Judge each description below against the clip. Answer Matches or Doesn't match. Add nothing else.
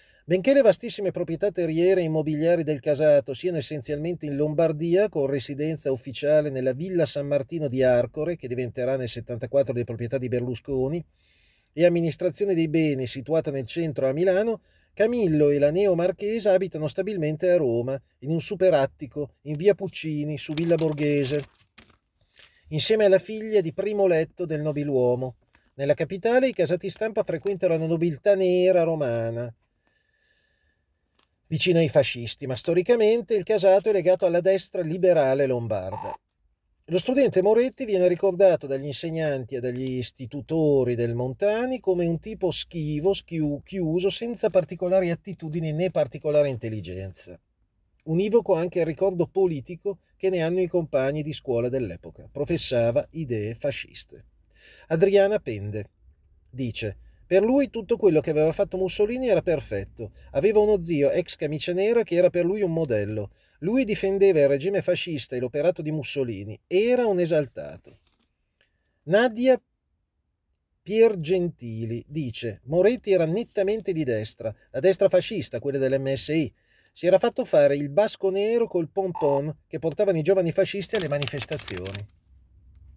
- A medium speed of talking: Matches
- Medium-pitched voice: Matches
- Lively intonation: Matches